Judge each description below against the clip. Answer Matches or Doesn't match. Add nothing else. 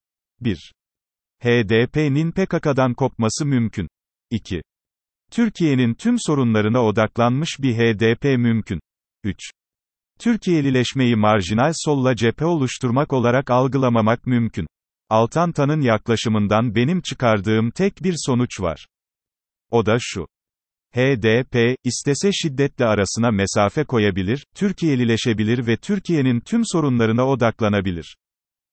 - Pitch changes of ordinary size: Matches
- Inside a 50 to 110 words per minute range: Matches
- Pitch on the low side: Matches